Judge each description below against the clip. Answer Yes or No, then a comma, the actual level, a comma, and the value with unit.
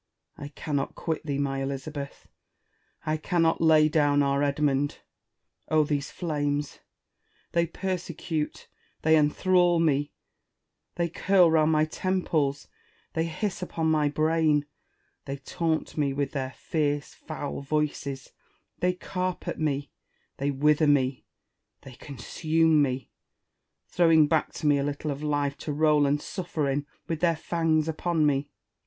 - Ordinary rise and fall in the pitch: No, narrow, 2.3 semitones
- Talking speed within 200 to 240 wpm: No, slow, 135 wpm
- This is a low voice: No, medium, 150 Hz